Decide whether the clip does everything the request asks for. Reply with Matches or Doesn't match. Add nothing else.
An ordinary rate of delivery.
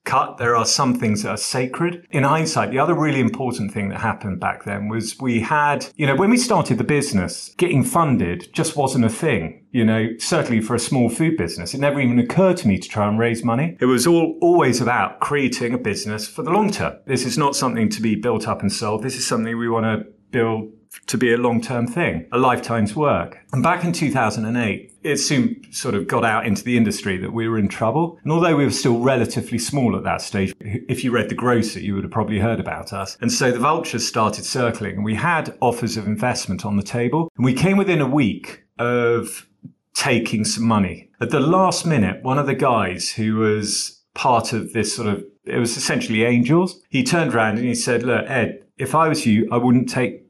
Doesn't match